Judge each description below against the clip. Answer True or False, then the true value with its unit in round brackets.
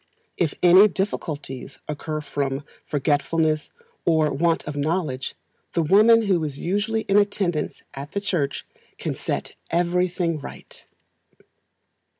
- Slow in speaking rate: True (120 wpm)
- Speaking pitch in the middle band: True (165 Hz)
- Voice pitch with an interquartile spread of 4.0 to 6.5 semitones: True (4.3 semitones)